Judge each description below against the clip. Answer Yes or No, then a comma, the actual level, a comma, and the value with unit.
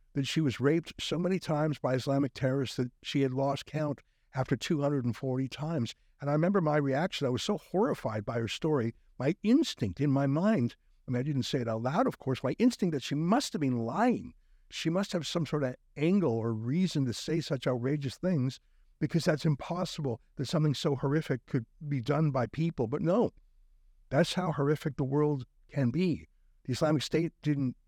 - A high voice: No, medium, 140 Hz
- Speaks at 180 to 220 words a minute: Yes, average, 200 wpm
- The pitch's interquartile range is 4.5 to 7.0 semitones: No, average, 3.9 semitones